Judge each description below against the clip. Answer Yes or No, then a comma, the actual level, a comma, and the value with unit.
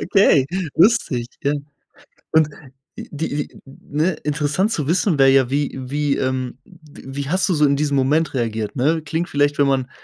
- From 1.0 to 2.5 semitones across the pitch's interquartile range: No, average, 2.9 semitones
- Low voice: No, medium, 145 Hz